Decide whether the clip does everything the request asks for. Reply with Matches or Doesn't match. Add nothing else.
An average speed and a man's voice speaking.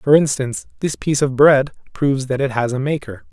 Doesn't match